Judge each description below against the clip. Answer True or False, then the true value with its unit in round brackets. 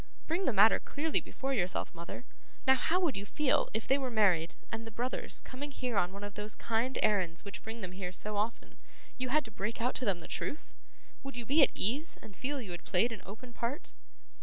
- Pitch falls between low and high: False (230 Hz)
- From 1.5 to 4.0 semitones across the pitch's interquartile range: False (4.7 semitones)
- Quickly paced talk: True (235 wpm)